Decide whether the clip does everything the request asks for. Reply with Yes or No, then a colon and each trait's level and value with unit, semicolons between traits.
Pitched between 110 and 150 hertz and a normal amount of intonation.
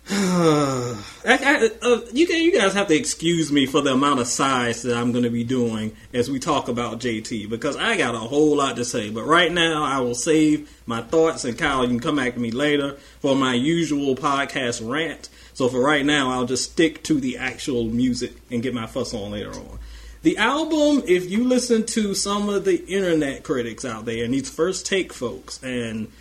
No: medium, 140 Hz; wide, 5.7 semitones